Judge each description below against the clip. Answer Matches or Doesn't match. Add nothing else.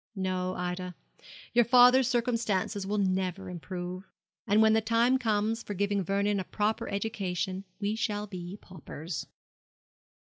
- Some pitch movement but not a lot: Matches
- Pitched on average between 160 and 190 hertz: Doesn't match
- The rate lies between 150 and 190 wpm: Doesn't match